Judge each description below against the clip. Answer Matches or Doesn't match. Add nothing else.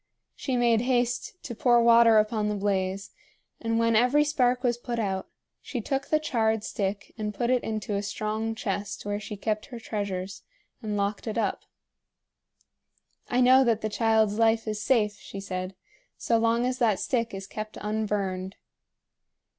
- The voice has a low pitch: Doesn't match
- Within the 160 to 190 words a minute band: Matches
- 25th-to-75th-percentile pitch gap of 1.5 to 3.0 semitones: Matches